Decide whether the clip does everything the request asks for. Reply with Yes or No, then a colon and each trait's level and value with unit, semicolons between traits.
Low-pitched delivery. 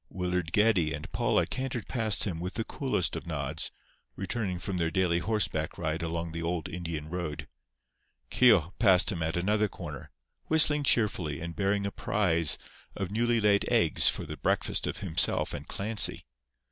Yes: very low, 90 Hz